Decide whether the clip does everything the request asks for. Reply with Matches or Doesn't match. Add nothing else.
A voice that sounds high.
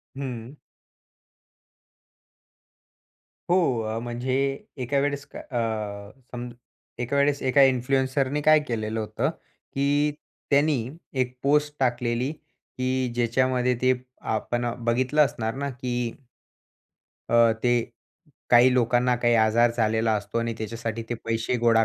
Doesn't match